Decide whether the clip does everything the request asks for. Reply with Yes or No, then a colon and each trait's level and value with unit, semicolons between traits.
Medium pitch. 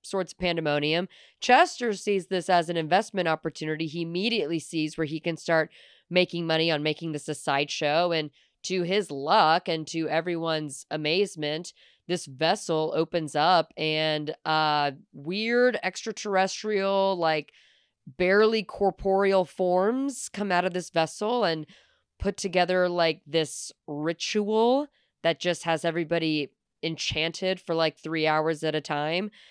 Yes: medium, 170 Hz